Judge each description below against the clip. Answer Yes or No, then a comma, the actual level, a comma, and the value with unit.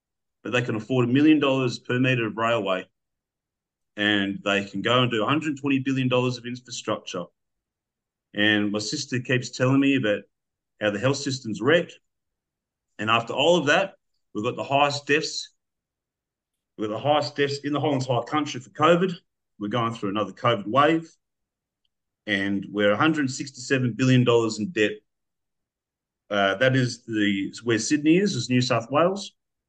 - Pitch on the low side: Yes, low, 125 Hz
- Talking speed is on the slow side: No, average, 160 wpm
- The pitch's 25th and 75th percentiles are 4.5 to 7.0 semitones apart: Yes, average, 4.9 semitones